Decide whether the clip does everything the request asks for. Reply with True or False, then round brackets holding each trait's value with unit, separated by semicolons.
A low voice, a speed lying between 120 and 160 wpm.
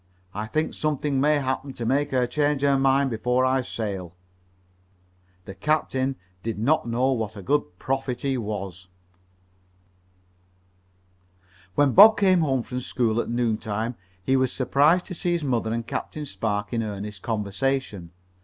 True (130 Hz; 155 wpm)